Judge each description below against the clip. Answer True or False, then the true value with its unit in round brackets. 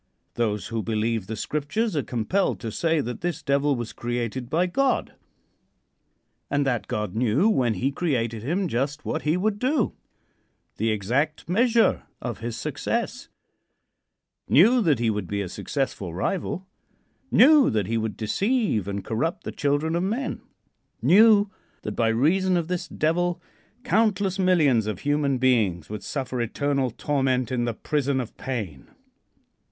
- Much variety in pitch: True (7.6 semitones)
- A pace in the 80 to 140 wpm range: False (150 wpm)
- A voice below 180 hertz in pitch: True (135 Hz)